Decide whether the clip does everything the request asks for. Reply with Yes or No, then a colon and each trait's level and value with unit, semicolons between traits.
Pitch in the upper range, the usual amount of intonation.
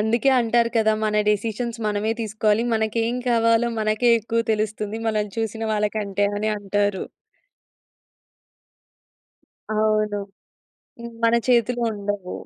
No: high, 215 Hz; narrow, 1.6 semitones